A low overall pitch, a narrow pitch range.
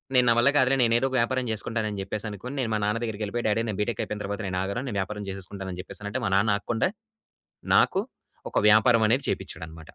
No: low, 105 Hz; average, 3.0 semitones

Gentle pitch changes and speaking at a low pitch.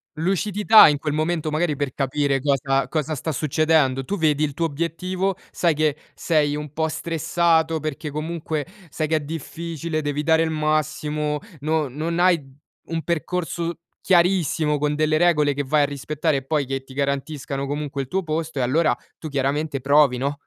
No: narrow, 2.2 semitones; medium, 155 Hz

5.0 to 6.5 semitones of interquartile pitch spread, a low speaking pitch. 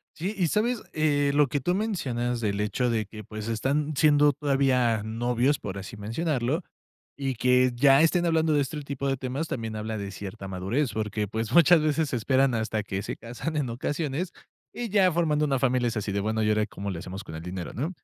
Yes: wide, 5.5 semitones; low, 130 Hz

